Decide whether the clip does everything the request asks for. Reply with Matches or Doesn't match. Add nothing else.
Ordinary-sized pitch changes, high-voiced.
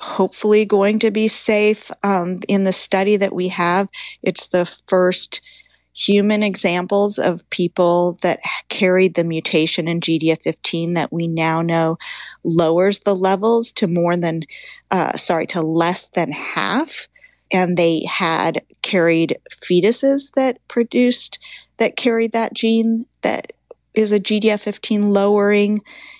Matches